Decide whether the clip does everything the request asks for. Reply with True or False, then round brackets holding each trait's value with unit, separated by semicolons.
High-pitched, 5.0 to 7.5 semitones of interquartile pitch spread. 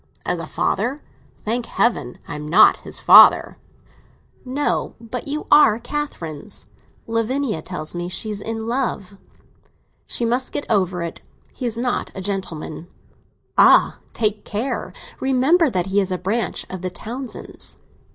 True (220 Hz; 5.4 semitones)